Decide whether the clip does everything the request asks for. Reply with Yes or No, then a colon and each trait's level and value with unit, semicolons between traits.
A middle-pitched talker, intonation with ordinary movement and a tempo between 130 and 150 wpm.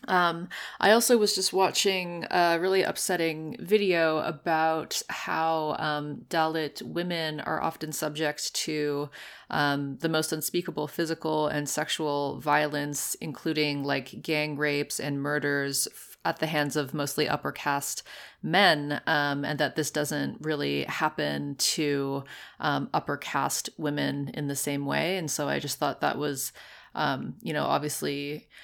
No: medium, 150 Hz; narrow, 2.0 semitones; average, 145 wpm